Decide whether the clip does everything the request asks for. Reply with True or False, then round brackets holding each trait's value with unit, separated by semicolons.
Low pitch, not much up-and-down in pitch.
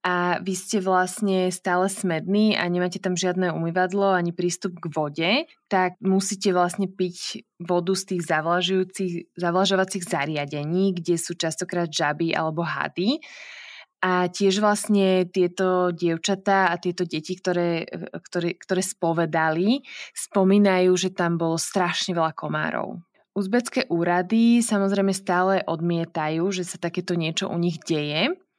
False (180 Hz; 2.1 semitones)